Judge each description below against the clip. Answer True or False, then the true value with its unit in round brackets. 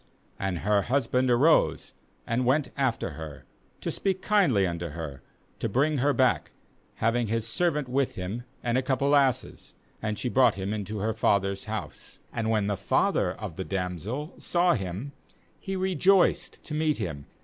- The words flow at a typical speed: True (170 wpm)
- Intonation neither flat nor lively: False (6.1 semitones)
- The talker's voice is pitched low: True (115 Hz)